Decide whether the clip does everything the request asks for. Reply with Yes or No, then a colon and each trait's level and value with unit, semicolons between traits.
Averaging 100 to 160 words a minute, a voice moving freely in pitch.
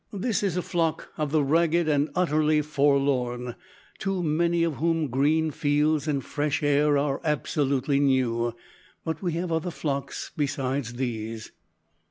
No: average, 145 wpm; average, 2.8 semitones